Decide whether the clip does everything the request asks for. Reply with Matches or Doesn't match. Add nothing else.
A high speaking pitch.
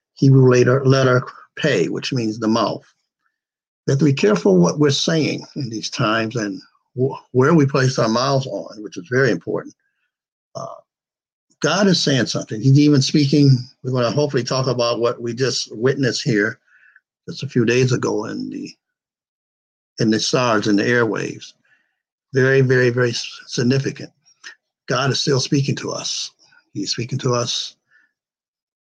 Doesn't match